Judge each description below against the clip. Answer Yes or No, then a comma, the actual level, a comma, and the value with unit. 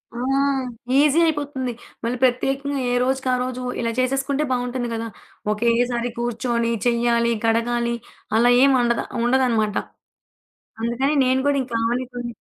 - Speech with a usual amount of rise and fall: No, narrow, 1.9 semitones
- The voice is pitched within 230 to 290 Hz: Yes, high, 245 Hz